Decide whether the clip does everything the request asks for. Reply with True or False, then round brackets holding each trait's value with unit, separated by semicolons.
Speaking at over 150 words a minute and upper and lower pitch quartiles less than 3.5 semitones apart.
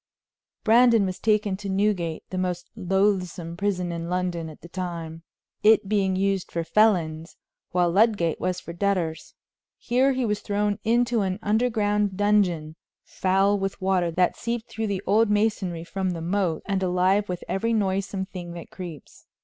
True (160 wpm; 2.9 semitones)